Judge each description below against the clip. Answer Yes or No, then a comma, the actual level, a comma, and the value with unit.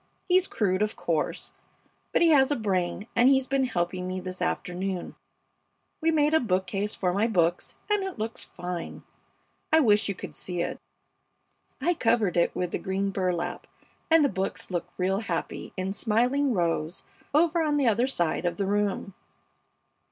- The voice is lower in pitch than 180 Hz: No, high, 200 Hz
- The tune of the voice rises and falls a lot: Yes, wide, 6.6 semitones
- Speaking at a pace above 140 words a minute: Yes, average, 170 wpm